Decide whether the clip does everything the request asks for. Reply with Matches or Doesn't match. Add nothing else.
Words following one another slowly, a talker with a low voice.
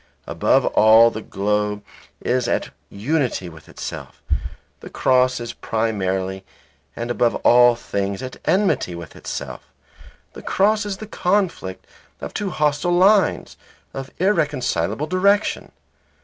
Matches